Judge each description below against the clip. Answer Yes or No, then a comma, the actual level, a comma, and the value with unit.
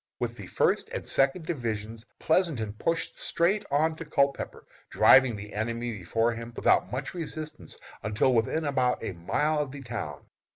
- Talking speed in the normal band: Yes, average, 160 wpm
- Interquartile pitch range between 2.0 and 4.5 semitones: No, wide, 5.5 semitones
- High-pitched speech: No, low, 130 Hz